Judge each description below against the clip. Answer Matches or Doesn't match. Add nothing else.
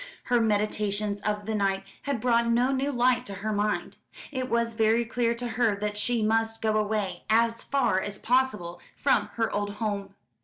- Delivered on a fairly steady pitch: Matches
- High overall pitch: Matches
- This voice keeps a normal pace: Matches